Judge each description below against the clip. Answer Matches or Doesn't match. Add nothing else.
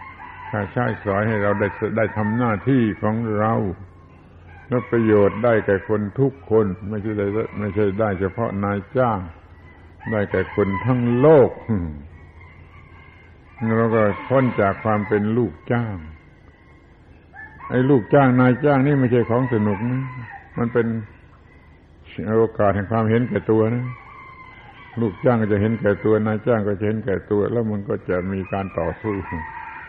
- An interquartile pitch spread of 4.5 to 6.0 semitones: Doesn't match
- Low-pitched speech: Matches